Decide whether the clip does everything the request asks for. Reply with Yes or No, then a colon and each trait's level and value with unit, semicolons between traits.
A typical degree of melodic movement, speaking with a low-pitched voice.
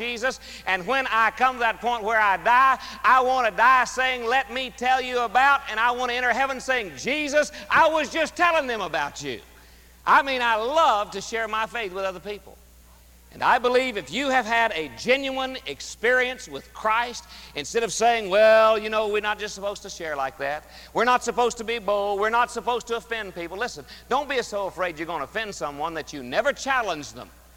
No: average, 5.0 semitones; high, 230 Hz